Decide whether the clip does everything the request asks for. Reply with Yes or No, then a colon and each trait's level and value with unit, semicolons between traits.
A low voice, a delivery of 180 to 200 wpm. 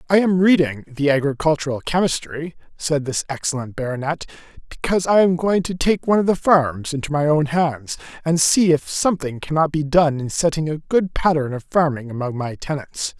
No: medium, 155 Hz; average, 185 wpm